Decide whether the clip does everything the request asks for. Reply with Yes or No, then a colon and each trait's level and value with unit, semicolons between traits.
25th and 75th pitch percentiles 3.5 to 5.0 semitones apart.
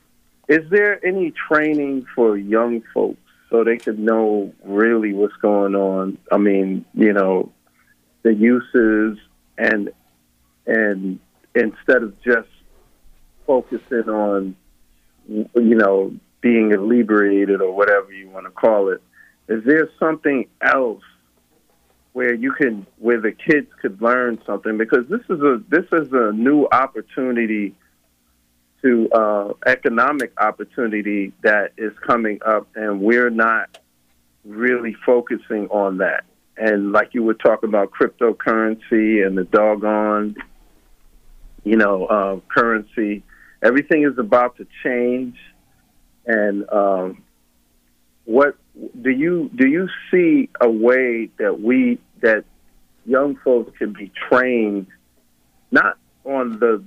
Yes: average, 3.9 semitones